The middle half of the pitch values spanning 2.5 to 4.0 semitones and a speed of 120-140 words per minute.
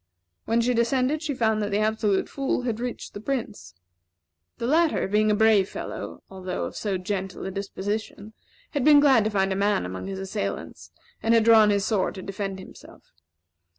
No: average, 3.3 semitones; average, 185 wpm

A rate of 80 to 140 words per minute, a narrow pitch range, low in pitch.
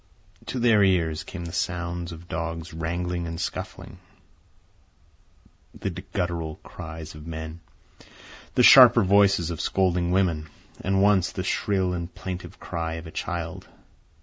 Yes: slow, 135 wpm; narrow, 2.1 semitones; very low, 85 Hz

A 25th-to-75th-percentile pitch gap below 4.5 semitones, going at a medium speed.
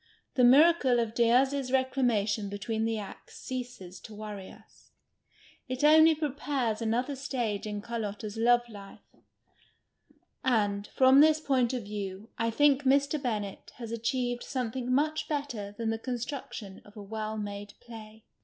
Yes: average, 3.7 semitones; average, 145 wpm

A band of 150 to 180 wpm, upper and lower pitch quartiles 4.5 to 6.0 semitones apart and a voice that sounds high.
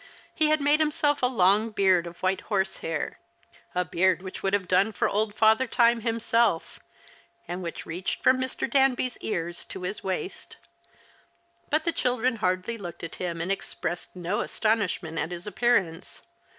Yes: average, 170 wpm; average, 5.0 semitones; high, 200 Hz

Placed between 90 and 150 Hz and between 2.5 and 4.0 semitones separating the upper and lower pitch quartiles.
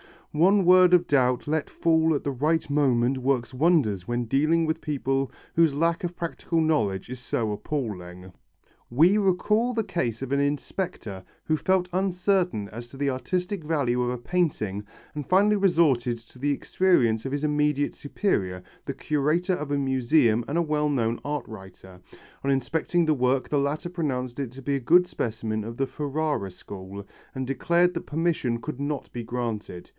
No: medium, 140 Hz; wide, 5.5 semitones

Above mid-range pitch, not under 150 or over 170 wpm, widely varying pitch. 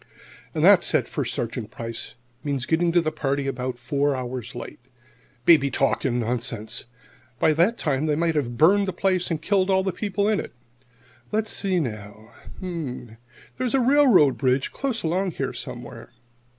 No: medium, 150 Hz; average, 165 wpm; wide, 7.0 semitones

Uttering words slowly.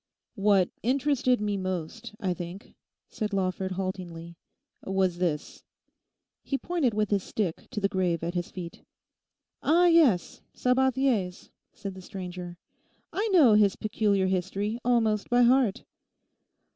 Yes: slow, 130 wpm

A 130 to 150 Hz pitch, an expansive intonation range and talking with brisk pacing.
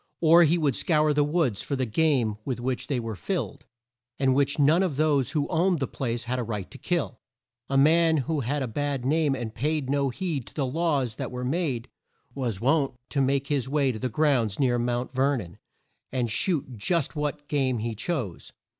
No: low, 135 Hz; average, 3.7 semitones; fast, 210 wpm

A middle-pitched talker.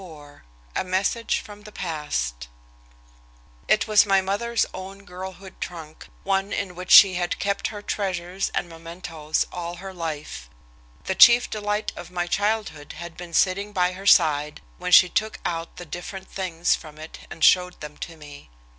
Yes: medium, 180 Hz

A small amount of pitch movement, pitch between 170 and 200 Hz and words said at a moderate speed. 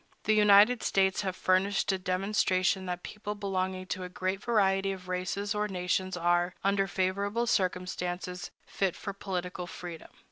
Yes: narrow, 1.7 semitones; high, 190 Hz; average, 150 wpm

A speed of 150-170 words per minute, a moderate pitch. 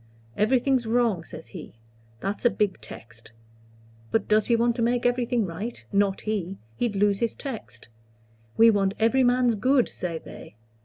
No: average, 160 wpm; high, 220 Hz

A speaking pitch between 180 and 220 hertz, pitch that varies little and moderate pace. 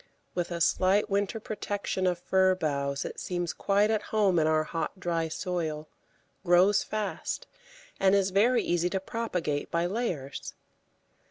No: medium, 185 Hz; average, 3.2 semitones; average, 150 wpm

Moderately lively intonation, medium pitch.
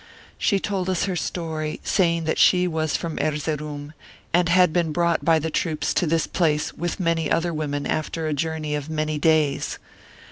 No: narrow, 2.0 semitones; medium, 160 Hz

